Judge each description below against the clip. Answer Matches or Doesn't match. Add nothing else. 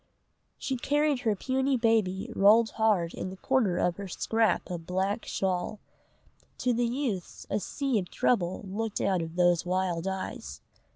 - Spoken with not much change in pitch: Doesn't match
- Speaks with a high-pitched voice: Matches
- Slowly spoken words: Doesn't match